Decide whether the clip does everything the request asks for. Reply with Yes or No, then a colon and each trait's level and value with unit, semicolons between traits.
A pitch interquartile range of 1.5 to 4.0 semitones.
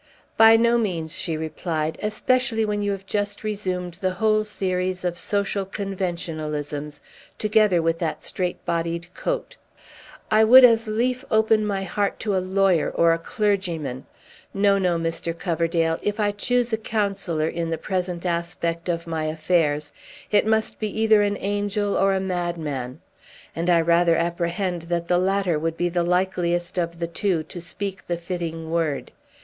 Yes: average, 3.5 semitones